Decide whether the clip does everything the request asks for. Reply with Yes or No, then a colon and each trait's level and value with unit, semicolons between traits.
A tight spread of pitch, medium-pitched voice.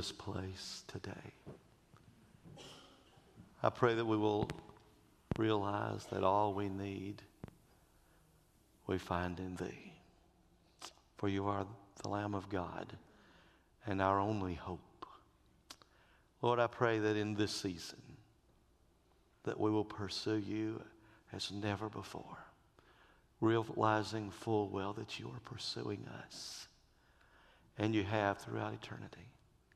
No: narrow, 1.9 semitones; low, 105 Hz